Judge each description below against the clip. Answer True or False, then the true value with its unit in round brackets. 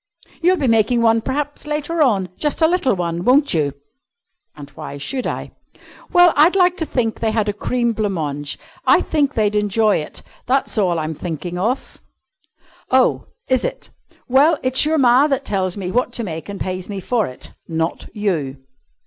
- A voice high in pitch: True (225 Hz)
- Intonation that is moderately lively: False (7.3 semitones)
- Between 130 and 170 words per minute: False (185 wpm)